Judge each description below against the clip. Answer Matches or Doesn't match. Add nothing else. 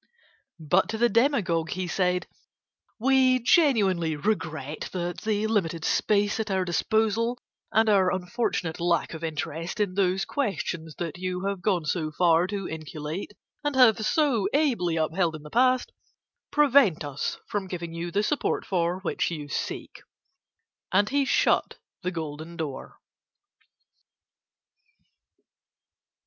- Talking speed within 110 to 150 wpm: Matches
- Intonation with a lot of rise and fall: Doesn't match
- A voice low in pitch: Doesn't match